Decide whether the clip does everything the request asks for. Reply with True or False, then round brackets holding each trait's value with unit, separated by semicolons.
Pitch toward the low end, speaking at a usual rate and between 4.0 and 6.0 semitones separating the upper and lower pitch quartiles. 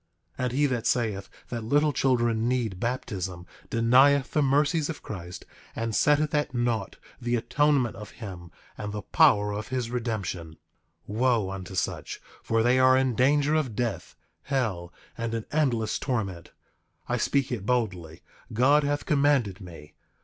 True (120 Hz; 155 wpm; 4.5 semitones)